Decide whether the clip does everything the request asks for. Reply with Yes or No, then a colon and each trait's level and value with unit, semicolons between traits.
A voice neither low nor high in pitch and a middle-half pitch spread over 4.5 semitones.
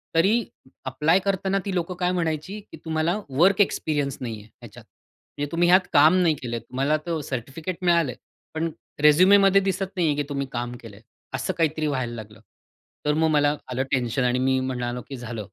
Yes: medium, 150 Hz; wide, 5.4 semitones